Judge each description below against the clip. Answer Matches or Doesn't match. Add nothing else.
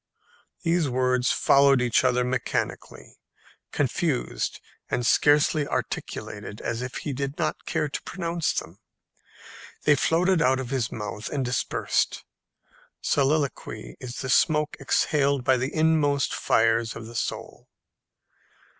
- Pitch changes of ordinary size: Matches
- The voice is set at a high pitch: Doesn't match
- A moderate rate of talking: Doesn't match